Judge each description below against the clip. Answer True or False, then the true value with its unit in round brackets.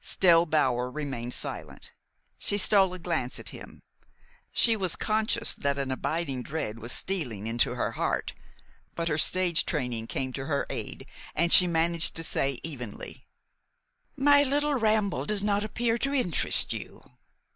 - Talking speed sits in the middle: True (155 wpm)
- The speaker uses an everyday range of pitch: False (7.3 semitones)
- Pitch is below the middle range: False (165 Hz)